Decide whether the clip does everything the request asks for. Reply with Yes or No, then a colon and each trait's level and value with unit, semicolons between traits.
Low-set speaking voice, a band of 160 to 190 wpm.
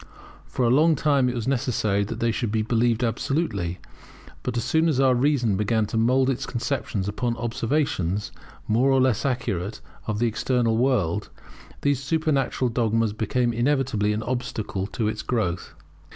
Yes: low, 120 Hz; average, 165 wpm